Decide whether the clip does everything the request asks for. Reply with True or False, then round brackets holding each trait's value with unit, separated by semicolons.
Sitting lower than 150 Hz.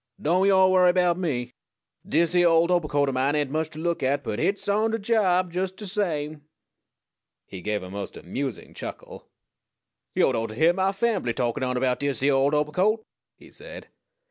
False (160 Hz)